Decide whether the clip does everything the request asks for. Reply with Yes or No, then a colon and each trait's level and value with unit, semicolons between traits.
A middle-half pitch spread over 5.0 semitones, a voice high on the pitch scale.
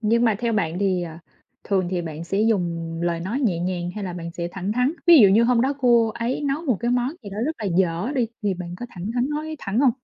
Yes: wide, 5.6 semitones; high, 205 Hz